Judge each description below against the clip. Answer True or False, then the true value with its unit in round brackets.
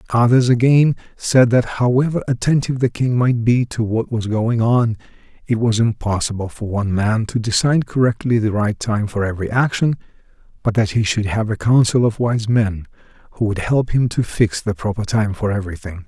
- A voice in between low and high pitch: False (115 Hz)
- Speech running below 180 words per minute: False (190 wpm)